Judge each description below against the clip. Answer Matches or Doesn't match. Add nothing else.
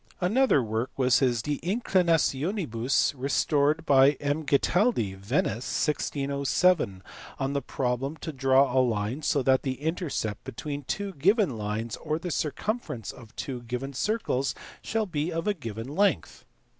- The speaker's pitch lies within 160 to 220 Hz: Doesn't match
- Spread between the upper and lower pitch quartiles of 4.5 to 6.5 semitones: Matches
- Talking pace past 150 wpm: Doesn't match